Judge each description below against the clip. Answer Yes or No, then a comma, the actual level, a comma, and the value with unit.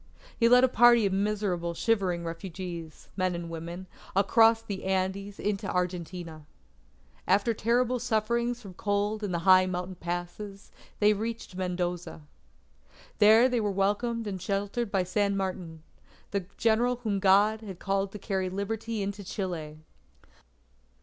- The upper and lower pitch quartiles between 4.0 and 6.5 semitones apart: No, average, 3.2 semitones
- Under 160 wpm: Yes, average, 140 wpm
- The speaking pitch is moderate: No, high, 195 Hz